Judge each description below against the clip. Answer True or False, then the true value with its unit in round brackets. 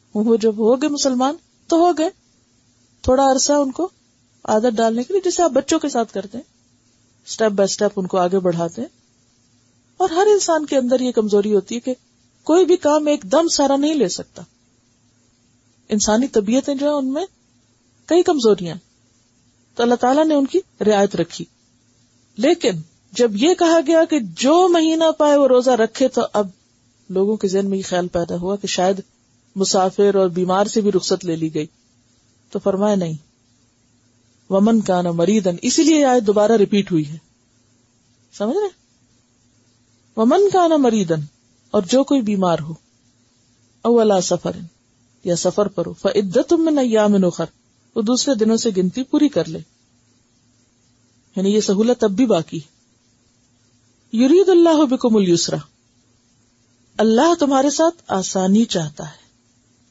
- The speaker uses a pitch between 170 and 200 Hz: True (195 Hz)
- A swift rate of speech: False (160 wpm)